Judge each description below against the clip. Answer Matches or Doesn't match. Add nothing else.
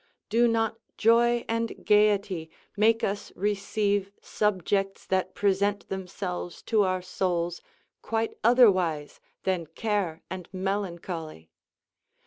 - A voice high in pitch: Matches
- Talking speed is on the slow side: Matches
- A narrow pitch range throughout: Doesn't match